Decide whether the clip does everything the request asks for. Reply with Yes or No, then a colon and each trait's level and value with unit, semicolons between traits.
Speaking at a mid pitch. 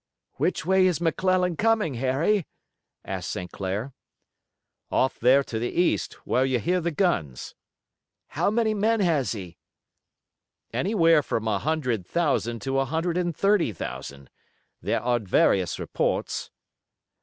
Yes: medium, 145 Hz